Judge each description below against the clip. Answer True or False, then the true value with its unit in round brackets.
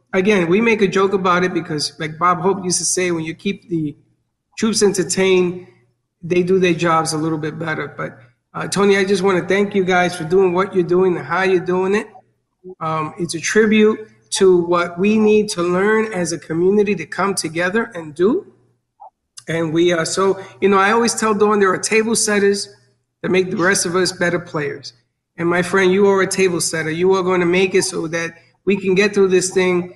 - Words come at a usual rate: False (220 wpm)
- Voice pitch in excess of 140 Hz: True (185 Hz)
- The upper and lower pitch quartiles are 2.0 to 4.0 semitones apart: True (2.6 semitones)